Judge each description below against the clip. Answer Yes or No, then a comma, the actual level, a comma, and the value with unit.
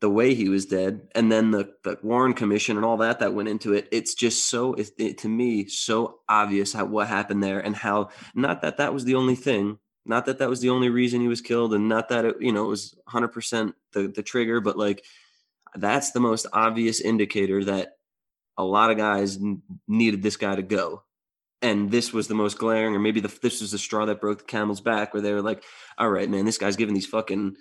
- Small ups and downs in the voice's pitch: Yes, narrow, 2.3 semitones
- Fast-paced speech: Yes, fast, 235 wpm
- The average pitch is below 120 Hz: Yes, low, 110 Hz